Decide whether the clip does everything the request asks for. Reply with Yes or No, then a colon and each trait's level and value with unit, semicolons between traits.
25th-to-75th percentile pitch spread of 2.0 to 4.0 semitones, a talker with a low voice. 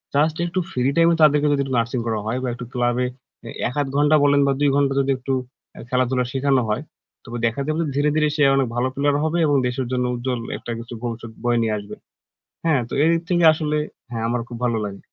Yes: average, 3.4 semitones; low, 130 Hz